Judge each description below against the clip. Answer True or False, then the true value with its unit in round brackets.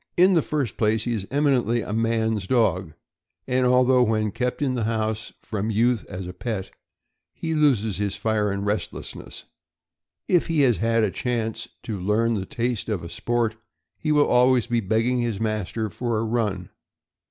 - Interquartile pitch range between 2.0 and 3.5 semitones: True (2.8 semitones)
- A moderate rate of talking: True (175 wpm)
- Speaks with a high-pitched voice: False (115 Hz)